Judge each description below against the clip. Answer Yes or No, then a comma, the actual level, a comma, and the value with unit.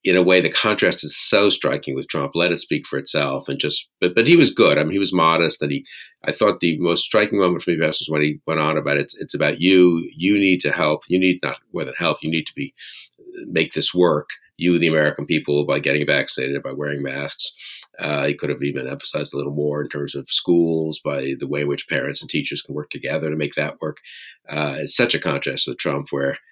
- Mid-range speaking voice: No, very low, 75 Hz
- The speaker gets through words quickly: Yes, fast, 250 wpm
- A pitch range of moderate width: Yes, average, 3.6 semitones